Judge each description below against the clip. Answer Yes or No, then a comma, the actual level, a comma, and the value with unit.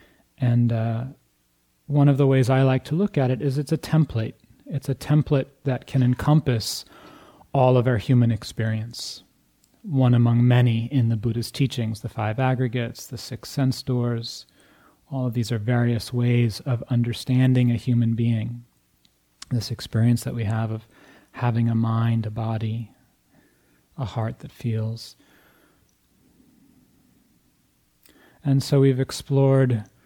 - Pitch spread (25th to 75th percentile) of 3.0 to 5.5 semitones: No, narrow, 2.6 semitones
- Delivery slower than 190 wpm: Yes, average, 140 wpm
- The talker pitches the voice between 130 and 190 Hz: No, low, 120 Hz